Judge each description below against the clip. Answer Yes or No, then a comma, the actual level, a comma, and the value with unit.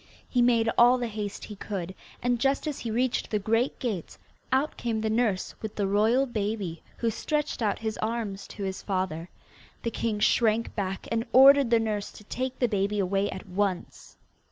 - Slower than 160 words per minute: No, average, 190 wpm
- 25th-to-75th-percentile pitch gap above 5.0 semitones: No, average, 3.1 semitones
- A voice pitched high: Yes, high, 220 Hz